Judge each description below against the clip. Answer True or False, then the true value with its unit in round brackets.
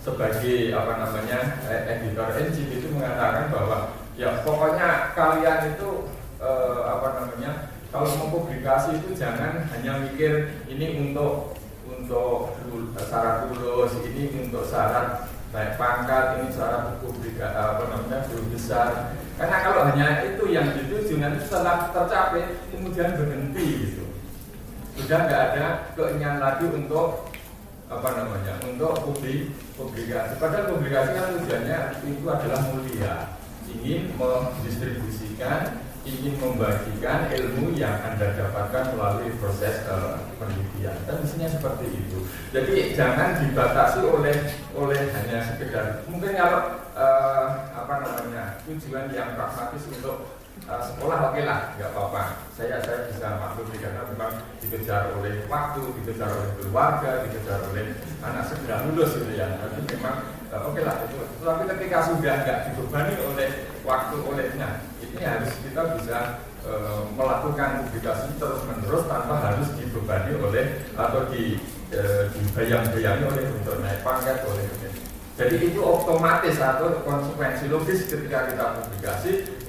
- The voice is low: True (130 Hz)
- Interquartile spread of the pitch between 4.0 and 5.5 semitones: True (4.8 semitones)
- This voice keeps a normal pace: True (125 wpm)